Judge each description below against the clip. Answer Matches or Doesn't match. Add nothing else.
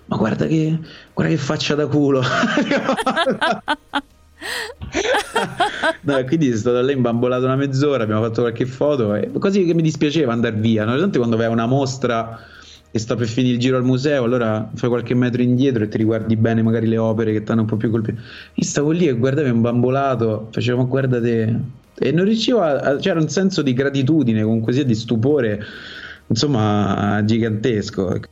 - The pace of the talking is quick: Matches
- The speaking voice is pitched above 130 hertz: Doesn't match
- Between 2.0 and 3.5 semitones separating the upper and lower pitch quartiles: Doesn't match